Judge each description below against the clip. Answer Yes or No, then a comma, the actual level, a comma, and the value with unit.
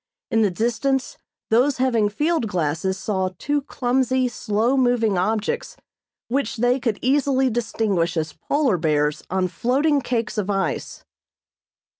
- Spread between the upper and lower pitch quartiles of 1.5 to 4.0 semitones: No, average, 5.2 semitones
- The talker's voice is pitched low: No, high, 230 Hz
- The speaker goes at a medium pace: No, slow, 130 wpm